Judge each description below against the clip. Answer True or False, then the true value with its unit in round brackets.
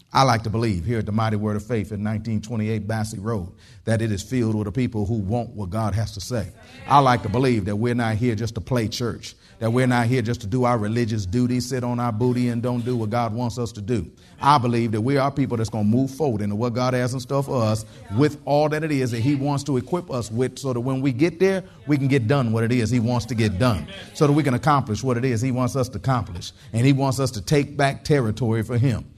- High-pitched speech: False (120 Hz)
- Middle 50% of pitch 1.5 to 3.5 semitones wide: True (2.8 semitones)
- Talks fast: True (280 wpm)